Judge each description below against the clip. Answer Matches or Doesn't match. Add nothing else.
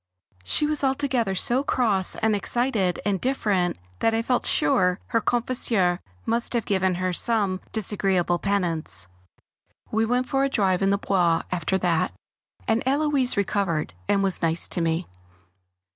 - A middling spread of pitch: Matches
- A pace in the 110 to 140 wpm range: Doesn't match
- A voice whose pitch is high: Matches